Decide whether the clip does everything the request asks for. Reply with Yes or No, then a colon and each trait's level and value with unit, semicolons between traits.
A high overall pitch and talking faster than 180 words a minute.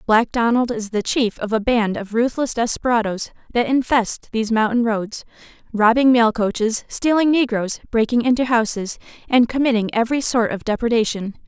No: high, 230 Hz; average, 155 wpm